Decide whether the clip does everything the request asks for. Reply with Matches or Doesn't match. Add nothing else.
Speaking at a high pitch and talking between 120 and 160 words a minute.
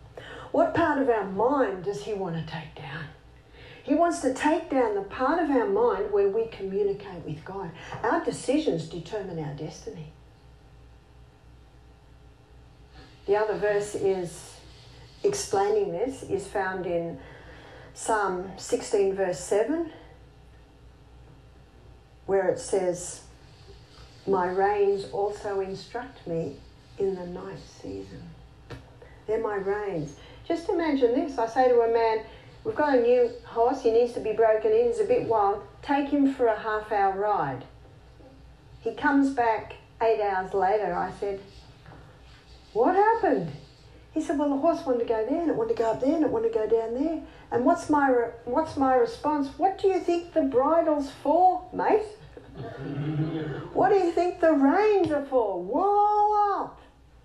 Matches